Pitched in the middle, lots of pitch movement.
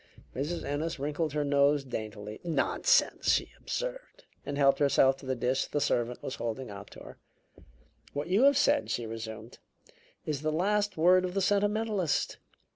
Yes: medium, 145 Hz; wide, 6.1 semitones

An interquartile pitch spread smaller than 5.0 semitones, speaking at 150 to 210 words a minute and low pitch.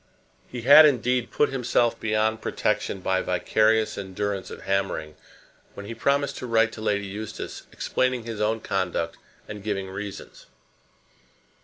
No: average, 3.2 semitones; average, 140 wpm; low, 110 Hz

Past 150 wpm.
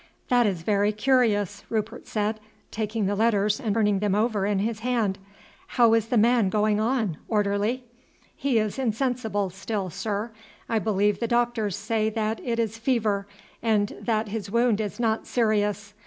Yes: average, 165 wpm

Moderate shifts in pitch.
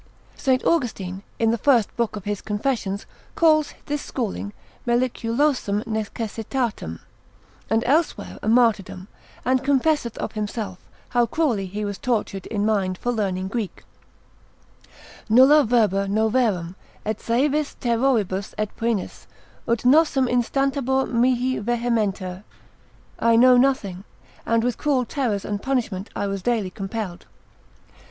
Yes: average, 4.0 semitones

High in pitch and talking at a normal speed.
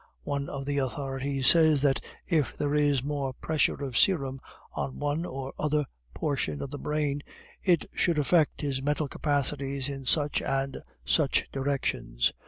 No: medium, 140 Hz; average, 155 wpm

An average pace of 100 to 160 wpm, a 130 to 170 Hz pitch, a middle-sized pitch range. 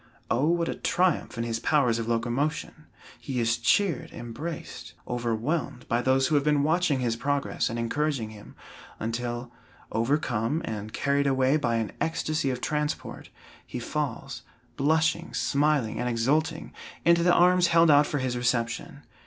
Yes: average, 155 wpm; low, 135 Hz; average, 4.5 semitones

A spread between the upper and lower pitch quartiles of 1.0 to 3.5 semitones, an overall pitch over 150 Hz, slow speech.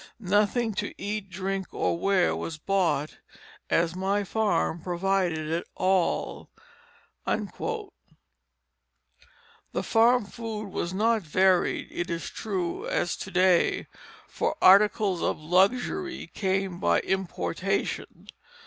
Yes: average, 3.2 semitones; high, 190 Hz; slow, 105 wpm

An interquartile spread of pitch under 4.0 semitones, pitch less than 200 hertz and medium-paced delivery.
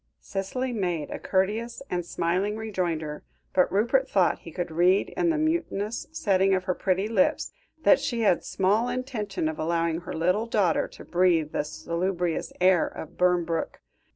No: average, 4.4 semitones; medium, 185 Hz; average, 160 wpm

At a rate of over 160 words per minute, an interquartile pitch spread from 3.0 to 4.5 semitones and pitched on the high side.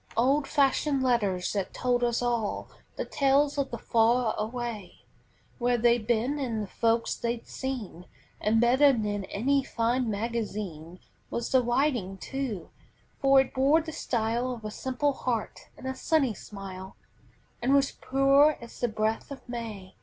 No: average, 155 wpm; average, 3.7 semitones; high, 240 Hz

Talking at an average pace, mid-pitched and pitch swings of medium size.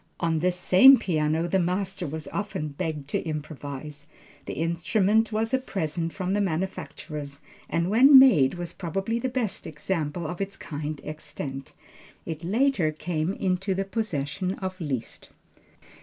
Yes: average, 145 wpm; medium, 175 Hz; average, 4.2 semitones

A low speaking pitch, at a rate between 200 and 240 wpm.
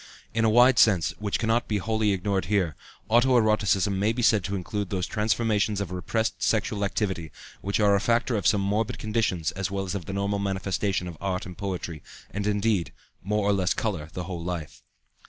Yes: low, 100 Hz; fast, 205 wpm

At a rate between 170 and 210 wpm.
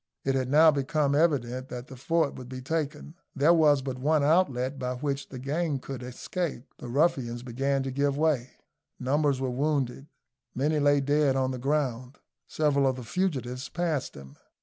Yes: average, 175 wpm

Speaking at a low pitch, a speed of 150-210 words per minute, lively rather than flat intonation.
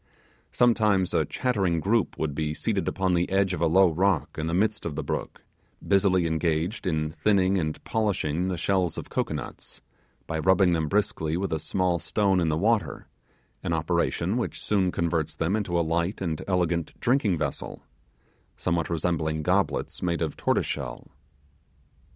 No: very low, 85 Hz; average, 165 wpm; average, 3.4 semitones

